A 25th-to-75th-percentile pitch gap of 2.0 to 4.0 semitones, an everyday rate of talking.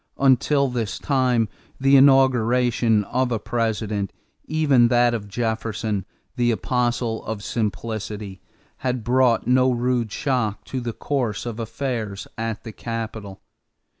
No: narrow, 2.6 semitones; slow, 125 wpm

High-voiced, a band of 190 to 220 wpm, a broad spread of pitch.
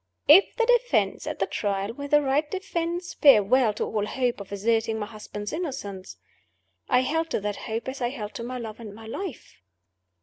Yes: high, 240 Hz; average, 195 wpm; wide, 6.0 semitones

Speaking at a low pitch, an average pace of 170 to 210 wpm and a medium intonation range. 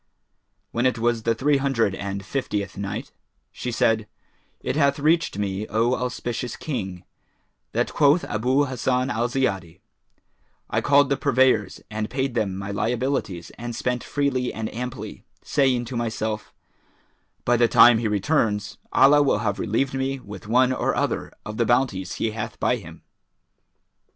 No: low, 120 Hz; average, 155 wpm; average, 3.8 semitones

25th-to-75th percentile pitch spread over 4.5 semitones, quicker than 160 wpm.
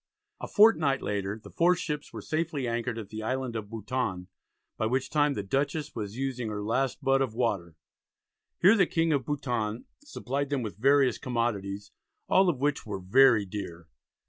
Yes: average, 5.1 semitones; average, 175 wpm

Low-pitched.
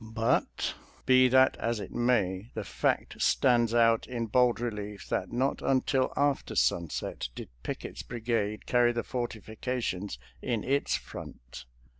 Yes: low, 115 Hz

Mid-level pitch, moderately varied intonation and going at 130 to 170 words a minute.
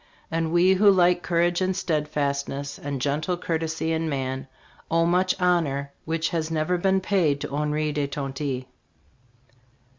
Yes: medium, 160 Hz; average, 3.6 semitones; average, 145 wpm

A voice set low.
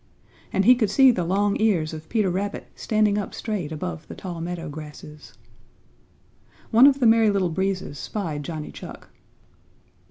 No: high, 190 Hz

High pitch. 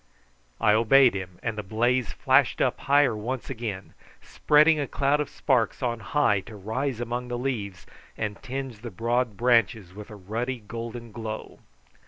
No: low, 115 Hz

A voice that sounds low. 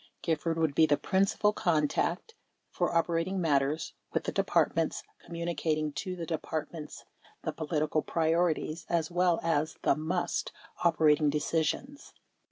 No: medium, 165 Hz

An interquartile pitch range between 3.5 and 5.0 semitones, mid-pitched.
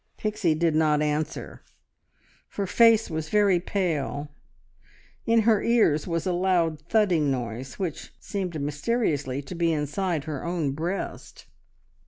Yes: average, 4.7 semitones; medium, 165 Hz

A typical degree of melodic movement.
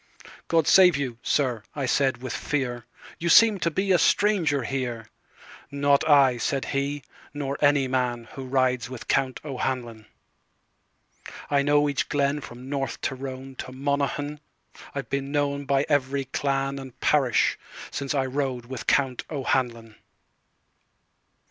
No: narrow, 1.9 semitones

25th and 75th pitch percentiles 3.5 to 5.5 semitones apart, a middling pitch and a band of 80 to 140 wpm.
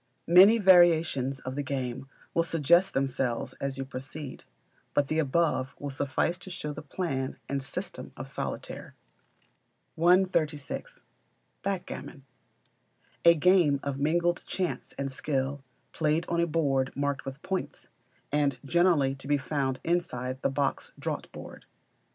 Yes: average, 4.1 semitones; medium, 145 Hz; slow, 135 wpm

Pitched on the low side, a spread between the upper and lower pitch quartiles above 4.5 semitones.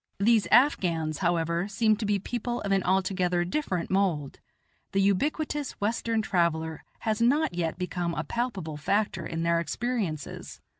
No: high, 195 Hz; average, 5.1 semitones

